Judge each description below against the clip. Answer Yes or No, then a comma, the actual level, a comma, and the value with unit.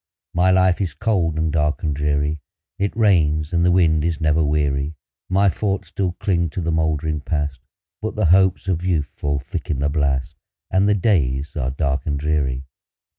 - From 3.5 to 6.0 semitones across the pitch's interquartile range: Yes, average, 3.8 semitones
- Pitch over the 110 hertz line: No, very low, 80 Hz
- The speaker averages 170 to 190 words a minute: Yes, average, 185 wpm